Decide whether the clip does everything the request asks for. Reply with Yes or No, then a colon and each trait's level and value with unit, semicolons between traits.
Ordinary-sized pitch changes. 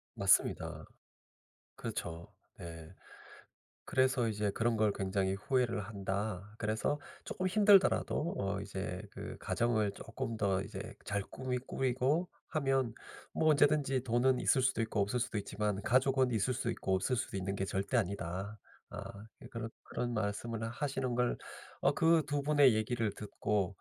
Yes: average, 4.6 semitones